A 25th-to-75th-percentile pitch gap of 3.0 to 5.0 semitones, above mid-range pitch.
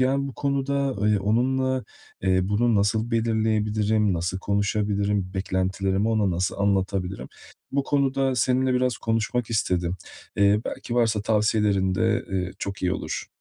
No: average, 3.8 semitones; low, 105 Hz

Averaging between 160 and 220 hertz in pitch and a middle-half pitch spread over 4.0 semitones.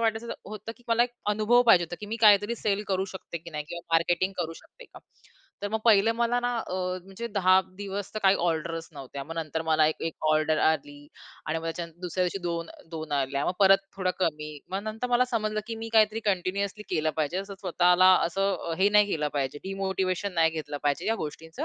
Yes: medium, 185 Hz; average, 4.4 semitones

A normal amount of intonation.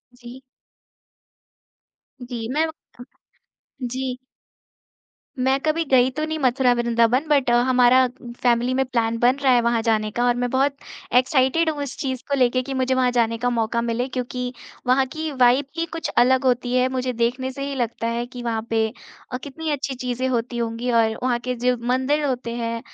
No: narrow, 1.8 semitones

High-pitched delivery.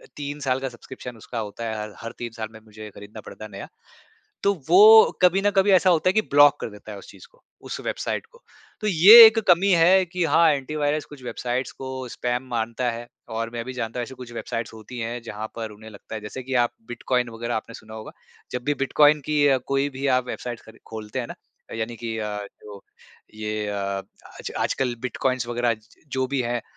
No: low, 120 Hz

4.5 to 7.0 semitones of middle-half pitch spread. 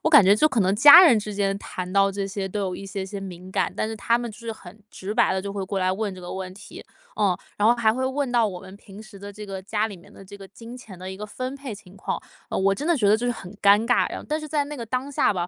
No: average, 3.3 semitones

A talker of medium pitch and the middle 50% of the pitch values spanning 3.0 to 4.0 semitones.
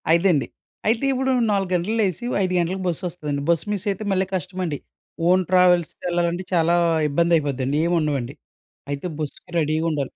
Yes: medium, 175 Hz; average, 3.5 semitones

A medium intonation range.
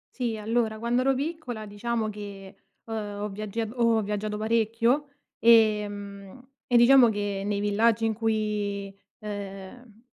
No: narrow, 2.2 semitones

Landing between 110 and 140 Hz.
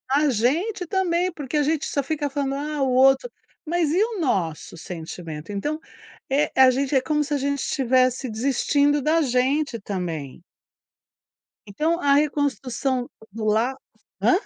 No: very high, 275 Hz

